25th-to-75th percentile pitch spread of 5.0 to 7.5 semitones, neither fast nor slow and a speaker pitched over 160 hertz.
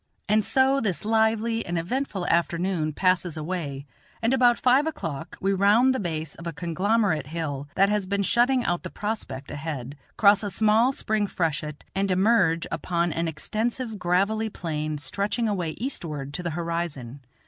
Yes: average, 5.3 semitones; average, 160 wpm; medium, 185 Hz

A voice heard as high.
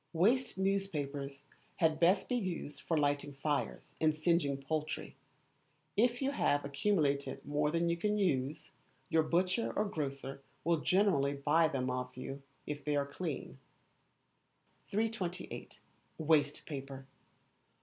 No: medium, 155 Hz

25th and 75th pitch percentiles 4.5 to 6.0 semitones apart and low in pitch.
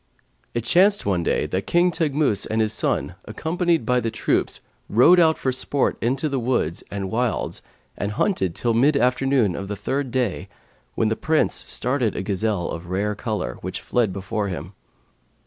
Yes: wide, 5.5 semitones; low, 115 Hz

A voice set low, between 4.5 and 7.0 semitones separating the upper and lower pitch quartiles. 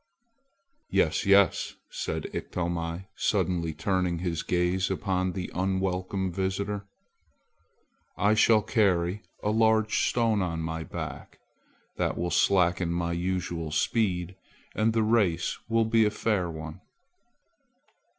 No: very low, 95 Hz; average, 3.2 semitones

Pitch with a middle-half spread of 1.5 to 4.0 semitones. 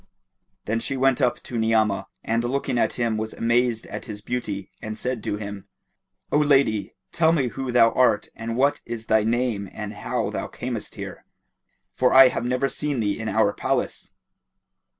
Yes: average, 2.8 semitones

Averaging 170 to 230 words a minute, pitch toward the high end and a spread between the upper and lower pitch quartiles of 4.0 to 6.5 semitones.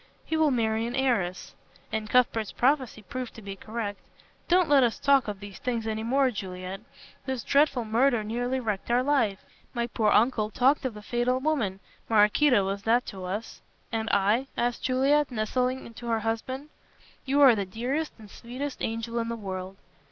No: average, 180 wpm; high, 235 Hz; average, 3.5 semitones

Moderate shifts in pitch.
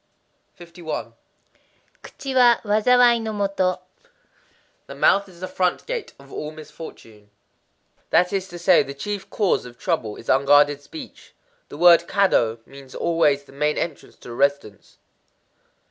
No: wide, 6.1 semitones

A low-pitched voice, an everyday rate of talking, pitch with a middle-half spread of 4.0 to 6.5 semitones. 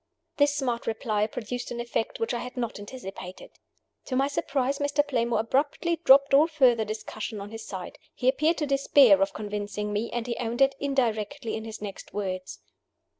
No: high, 240 Hz; average, 180 wpm; average, 4.4 semitones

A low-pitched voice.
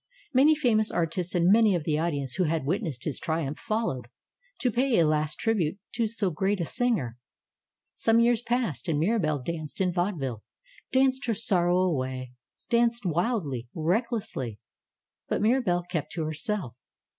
No: medium, 175 Hz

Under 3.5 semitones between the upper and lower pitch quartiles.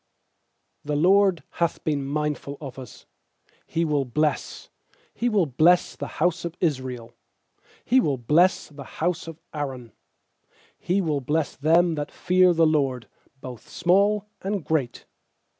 No: average, 4.1 semitones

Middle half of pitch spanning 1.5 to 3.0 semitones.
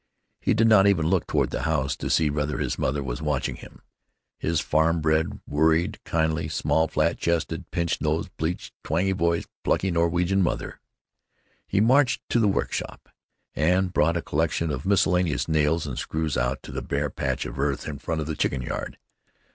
Yes: average, 2.7 semitones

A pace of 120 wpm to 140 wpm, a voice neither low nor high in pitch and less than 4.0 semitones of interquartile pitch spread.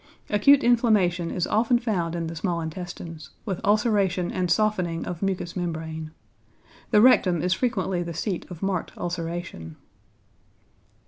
Yes: slow, 135 wpm; medium, 180 Hz; average, 3.6 semitones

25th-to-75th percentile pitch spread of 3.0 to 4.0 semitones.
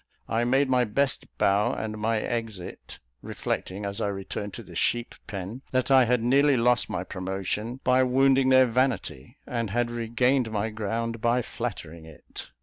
Yes: average, 3.5 semitones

